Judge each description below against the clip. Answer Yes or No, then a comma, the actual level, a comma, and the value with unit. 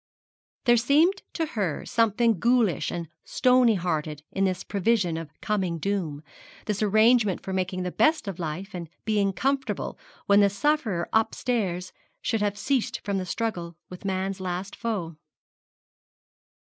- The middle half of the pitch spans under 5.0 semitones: Yes, average, 4.2 semitones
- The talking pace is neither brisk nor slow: Yes, average, 145 wpm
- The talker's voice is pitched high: Yes, high, 200 Hz